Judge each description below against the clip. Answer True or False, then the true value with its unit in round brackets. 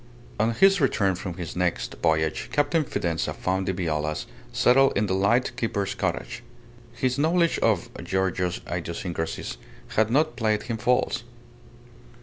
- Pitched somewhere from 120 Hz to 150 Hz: False (100 Hz)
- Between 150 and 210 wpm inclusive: False (135 wpm)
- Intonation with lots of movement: True (6.1 semitones)